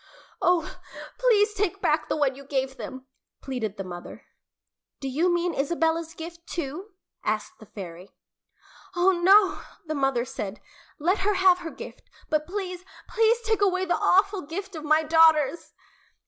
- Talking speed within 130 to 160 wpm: Yes, average, 155 wpm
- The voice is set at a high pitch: Yes, very high, 330 Hz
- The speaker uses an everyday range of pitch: No, wide, 5.7 semitones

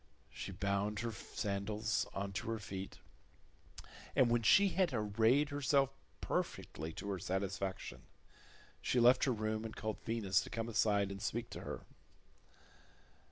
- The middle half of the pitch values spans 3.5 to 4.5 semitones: No, average, 3.1 semitones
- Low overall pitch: Yes, low, 110 Hz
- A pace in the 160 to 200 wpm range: No, average, 145 wpm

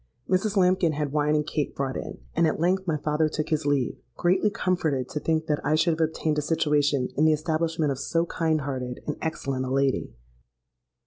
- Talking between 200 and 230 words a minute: Yes, fast, 205 wpm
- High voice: No, medium, 155 Hz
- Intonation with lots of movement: No, narrow, 2.4 semitones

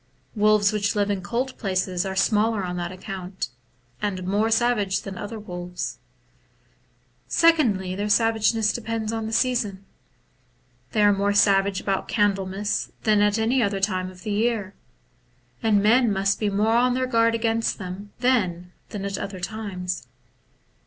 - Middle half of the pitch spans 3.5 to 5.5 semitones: No, average, 2.7 semitones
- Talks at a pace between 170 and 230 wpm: No, average, 150 wpm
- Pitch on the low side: No, high, 205 Hz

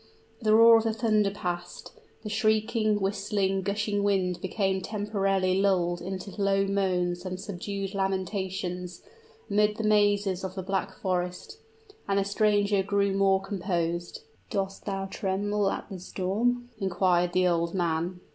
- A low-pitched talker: No, high, 195 Hz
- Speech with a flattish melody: Yes, narrow, 1.9 semitones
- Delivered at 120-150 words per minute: Yes, average, 140 wpm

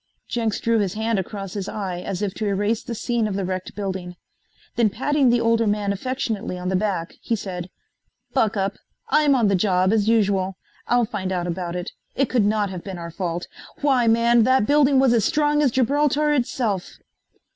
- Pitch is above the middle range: Yes, high, 210 Hz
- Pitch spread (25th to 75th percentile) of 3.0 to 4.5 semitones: Yes, average, 4.1 semitones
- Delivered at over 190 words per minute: Yes, average, 200 wpm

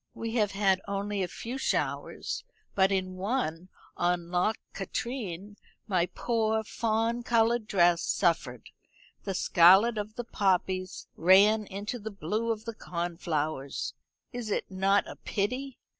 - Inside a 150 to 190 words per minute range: No, slow, 135 wpm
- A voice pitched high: Yes, high, 200 Hz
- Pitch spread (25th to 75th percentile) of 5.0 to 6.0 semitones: No, average, 3.4 semitones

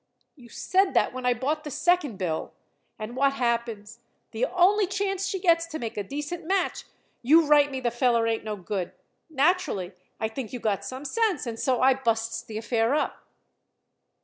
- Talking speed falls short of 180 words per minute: No, average, 185 wpm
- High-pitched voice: Yes, very high, 260 Hz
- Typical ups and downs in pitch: No, wide, 6.5 semitones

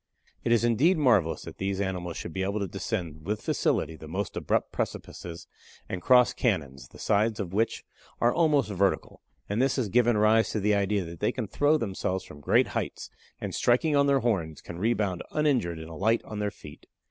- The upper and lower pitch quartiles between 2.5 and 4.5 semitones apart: No, average, 5.1 semitones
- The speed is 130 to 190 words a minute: No, average, 200 wpm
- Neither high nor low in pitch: No, low, 105 Hz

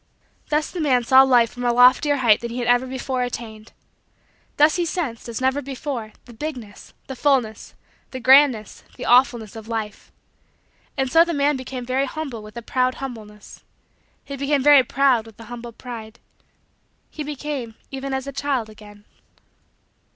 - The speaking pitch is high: Yes, very high, 255 Hz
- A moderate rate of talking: Yes, average, 170 wpm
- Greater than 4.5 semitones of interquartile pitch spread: No, average, 3.2 semitones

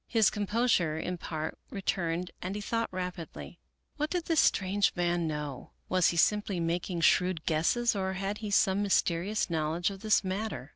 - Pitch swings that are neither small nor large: Yes, average, 3.6 semitones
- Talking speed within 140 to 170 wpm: Yes, average, 165 wpm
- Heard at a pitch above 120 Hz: Yes, medium, 185 Hz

